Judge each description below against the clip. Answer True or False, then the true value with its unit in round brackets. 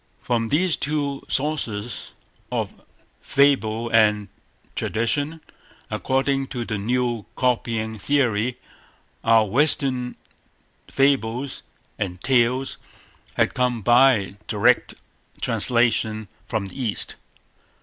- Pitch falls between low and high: False (120 Hz)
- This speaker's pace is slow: True (90 wpm)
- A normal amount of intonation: True (3.5 semitones)